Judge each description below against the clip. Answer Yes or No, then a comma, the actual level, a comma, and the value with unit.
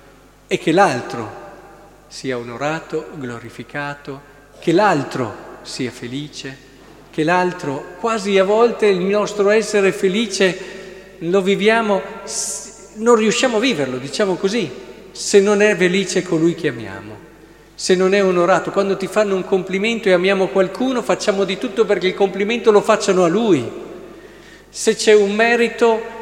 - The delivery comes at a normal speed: Yes, average, 135 wpm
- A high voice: Yes, high, 195 Hz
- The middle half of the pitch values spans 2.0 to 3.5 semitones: No, average, 4.1 semitones